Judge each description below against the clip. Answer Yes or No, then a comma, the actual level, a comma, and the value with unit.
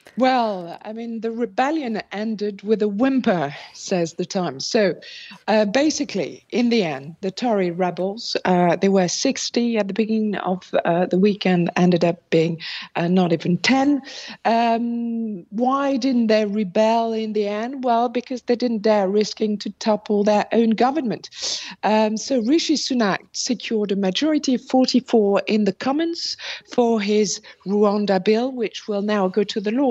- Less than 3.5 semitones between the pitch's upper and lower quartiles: No, average, 3.8 semitones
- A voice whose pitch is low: No, high, 215 Hz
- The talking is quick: No, average, 165 wpm